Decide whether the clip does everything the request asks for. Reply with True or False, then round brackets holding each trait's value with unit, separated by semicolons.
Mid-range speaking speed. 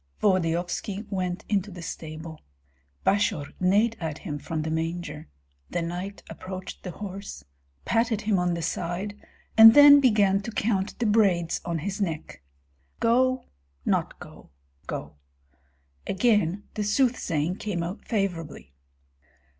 False (130 wpm)